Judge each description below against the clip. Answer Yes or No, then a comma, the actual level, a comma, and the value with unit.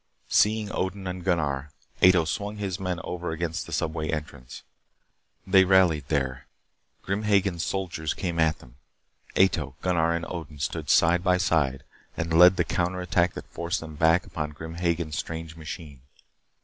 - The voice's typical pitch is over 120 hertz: No, very low, 85 Hz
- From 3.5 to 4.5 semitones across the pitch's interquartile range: No, average, 2.7 semitones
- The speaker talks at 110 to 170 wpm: Yes, average, 160 wpm